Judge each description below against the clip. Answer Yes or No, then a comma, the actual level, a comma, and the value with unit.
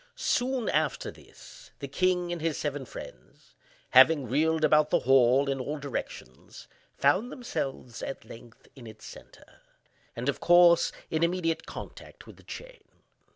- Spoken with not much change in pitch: No, average, 4.5 semitones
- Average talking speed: Yes, average, 150 wpm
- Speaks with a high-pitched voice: No, medium, 150 Hz